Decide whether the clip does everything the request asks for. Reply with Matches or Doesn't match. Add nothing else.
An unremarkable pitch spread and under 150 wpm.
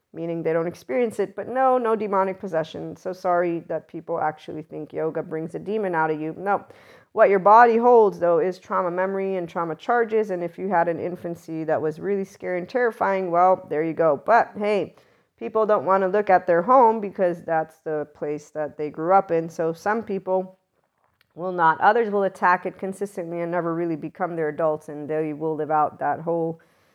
Doesn't match